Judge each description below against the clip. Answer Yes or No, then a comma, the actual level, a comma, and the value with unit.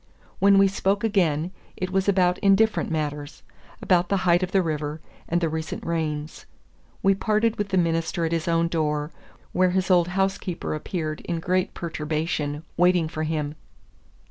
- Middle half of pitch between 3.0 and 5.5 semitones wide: Yes, average, 3.3 semitones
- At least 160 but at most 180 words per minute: Yes, average, 165 wpm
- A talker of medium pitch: Yes, medium, 175 Hz